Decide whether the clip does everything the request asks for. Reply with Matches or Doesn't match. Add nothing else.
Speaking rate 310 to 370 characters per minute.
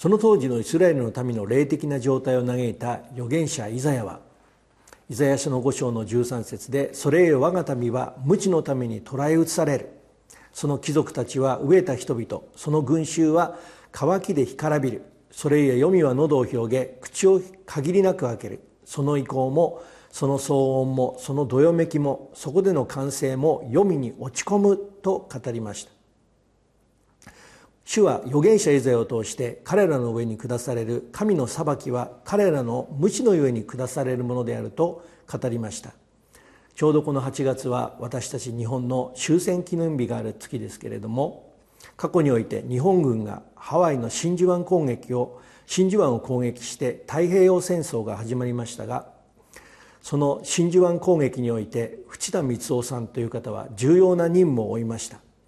Matches